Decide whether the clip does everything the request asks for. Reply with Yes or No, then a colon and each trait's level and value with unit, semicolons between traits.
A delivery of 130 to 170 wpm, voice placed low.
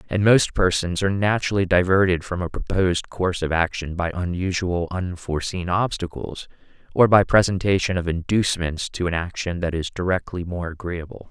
Yes: average, 155 wpm; very low, 90 Hz